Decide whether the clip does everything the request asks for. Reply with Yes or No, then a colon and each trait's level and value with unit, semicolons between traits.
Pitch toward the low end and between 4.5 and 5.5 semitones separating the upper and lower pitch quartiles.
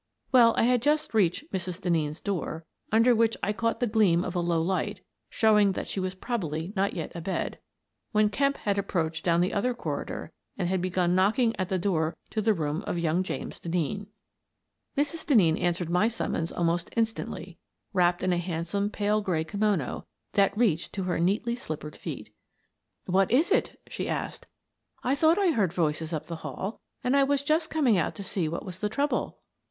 No: high, 195 Hz; average, 4.8 semitones